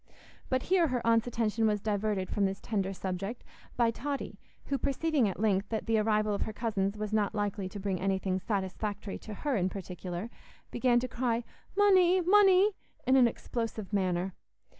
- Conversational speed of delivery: Yes, average, 175 wpm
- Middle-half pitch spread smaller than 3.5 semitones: No, average, 4.0 semitones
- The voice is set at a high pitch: Yes, high, 215 Hz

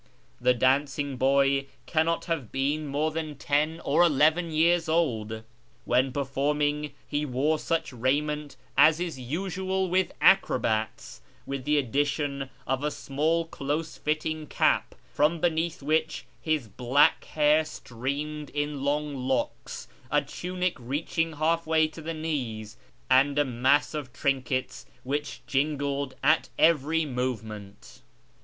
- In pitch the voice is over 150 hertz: No, medium, 145 Hz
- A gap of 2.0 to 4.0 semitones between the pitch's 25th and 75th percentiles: Yes, average, 2.9 semitones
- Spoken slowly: Yes, slow, 130 wpm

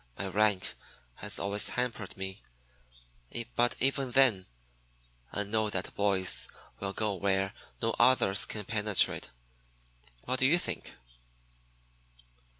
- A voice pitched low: Yes, low, 105 Hz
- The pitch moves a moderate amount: Yes, average, 3.5 semitones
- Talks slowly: Yes, slow, 115 wpm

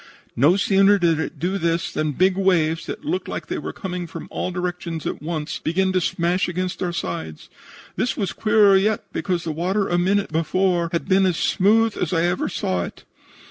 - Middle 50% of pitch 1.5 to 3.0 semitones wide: Yes, average, 2.7 semitones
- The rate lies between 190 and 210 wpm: Yes, average, 195 wpm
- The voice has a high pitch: No, medium, 180 Hz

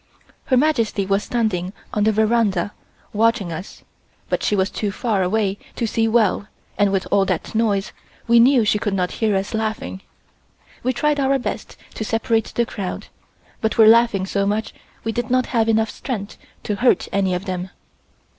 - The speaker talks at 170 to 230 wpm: Yes, average, 180 wpm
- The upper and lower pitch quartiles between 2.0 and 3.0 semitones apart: Yes, average, 2.7 semitones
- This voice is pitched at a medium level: No, high, 215 Hz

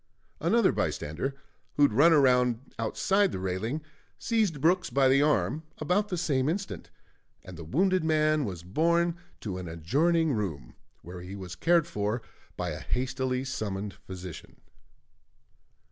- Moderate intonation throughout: No, wide, 9.0 semitones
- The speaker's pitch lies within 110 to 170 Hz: Yes, low, 135 Hz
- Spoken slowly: No, average, 145 wpm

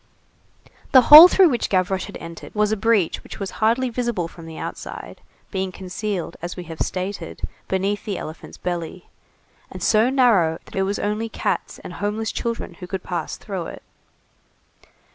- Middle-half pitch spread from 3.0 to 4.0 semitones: Yes, average, 3.7 semitones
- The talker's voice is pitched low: No, high, 195 Hz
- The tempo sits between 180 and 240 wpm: No, average, 170 wpm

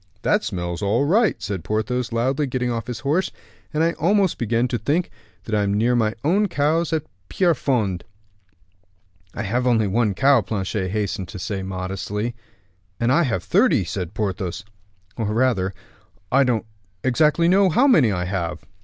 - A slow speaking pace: No, average, 160 wpm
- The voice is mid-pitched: No, low, 115 Hz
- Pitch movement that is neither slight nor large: No, wide, 6.1 semitones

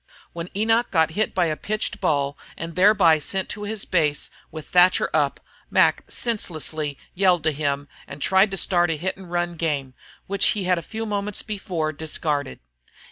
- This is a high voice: No, medium, 175 Hz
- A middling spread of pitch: Yes, average, 4.1 semitones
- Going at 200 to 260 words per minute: No, average, 180 wpm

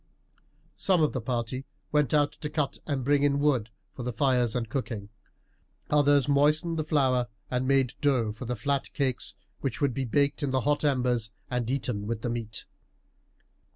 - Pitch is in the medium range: No, low, 130 Hz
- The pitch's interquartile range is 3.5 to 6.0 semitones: No, average, 3.1 semitones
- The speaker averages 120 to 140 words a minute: No, average, 180 wpm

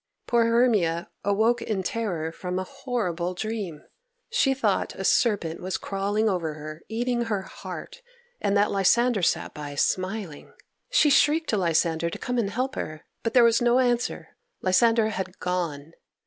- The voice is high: Yes, high, 205 Hz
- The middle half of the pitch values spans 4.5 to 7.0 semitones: Yes, average, 5.3 semitones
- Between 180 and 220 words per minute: No, average, 160 wpm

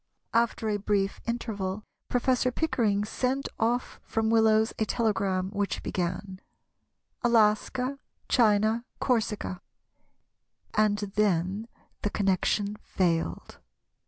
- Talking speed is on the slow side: Yes, slow, 90 wpm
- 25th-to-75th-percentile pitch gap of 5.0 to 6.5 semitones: No, average, 2.7 semitones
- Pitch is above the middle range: Yes, high, 215 Hz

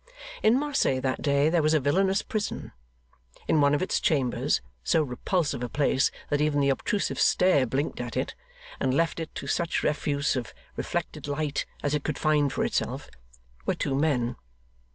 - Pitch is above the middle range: No, medium, 145 Hz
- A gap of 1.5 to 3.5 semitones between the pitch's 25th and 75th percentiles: Yes, average, 2.9 semitones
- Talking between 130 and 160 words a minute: No, average, 175 wpm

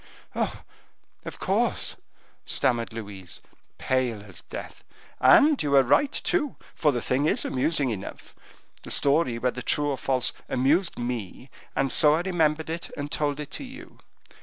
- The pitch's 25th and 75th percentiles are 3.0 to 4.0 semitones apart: No, average, 4.4 semitones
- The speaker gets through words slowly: No, average, 155 wpm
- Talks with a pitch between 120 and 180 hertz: Yes, low, 135 Hz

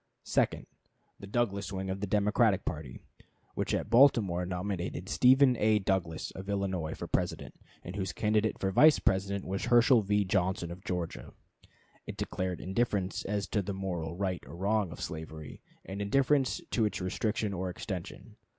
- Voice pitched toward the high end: No, very low, 95 Hz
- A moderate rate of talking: Yes, average, 160 wpm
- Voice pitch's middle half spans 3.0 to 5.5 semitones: No, narrow, 2.6 semitones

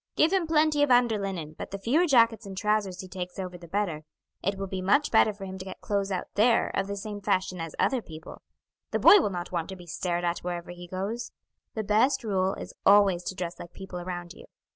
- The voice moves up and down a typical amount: Yes, average, 3.3 semitones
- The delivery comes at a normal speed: No, fast, 240 wpm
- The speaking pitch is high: Yes, high, 195 Hz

